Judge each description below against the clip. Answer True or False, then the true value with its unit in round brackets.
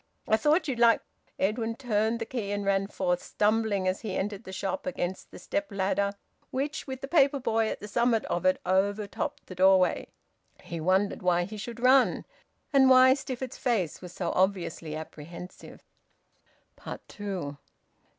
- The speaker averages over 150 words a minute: True (165 wpm)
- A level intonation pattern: False (4.6 semitones)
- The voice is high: True (205 Hz)